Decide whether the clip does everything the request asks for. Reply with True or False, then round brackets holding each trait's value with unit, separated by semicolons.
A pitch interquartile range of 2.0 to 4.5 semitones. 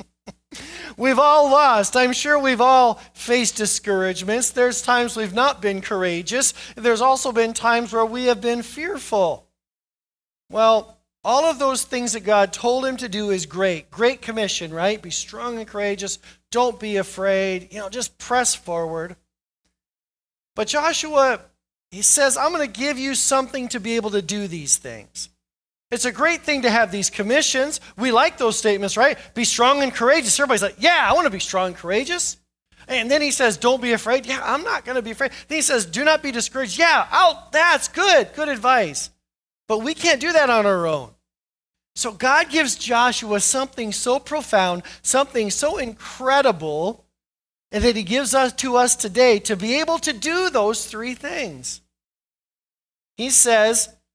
False (4.9 semitones)